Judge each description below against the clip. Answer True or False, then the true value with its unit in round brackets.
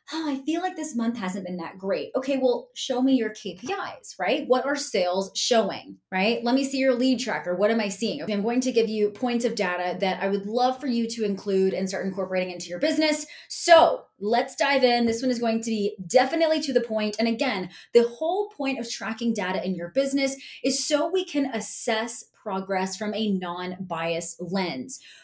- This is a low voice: False (230 Hz)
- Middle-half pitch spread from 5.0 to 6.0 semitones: True (5.4 semitones)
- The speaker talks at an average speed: False (215 wpm)